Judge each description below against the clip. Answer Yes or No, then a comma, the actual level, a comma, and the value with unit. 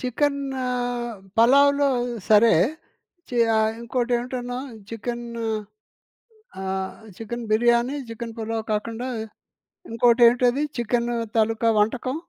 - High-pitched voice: Yes, high, 235 Hz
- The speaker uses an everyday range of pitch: No, narrow, 1.9 semitones